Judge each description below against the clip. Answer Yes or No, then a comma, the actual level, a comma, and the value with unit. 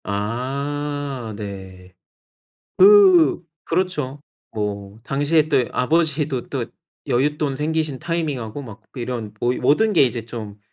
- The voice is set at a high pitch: No, low, 135 Hz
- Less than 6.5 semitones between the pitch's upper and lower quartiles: Yes, average, 5.2 semitones